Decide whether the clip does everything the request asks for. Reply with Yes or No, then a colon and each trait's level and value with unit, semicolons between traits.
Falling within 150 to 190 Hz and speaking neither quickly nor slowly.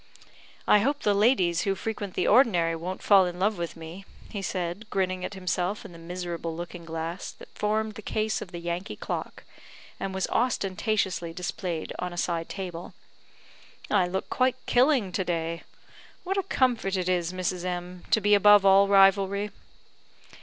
Yes: medium, 185 Hz; average, 170 wpm